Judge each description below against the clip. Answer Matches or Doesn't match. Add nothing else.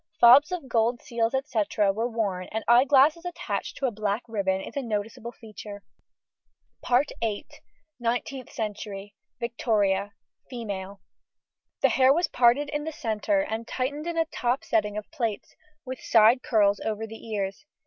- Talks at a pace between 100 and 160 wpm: Matches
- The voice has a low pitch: Doesn't match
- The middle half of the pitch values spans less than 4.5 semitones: Matches